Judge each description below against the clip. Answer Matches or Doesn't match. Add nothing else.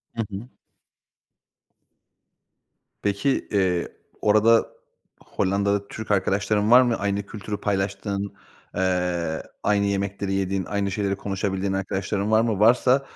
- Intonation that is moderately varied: Doesn't match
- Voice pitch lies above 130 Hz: Doesn't match